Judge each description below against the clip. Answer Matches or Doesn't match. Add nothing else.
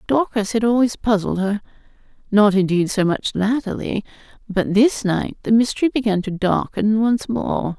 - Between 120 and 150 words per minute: Matches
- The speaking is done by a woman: Matches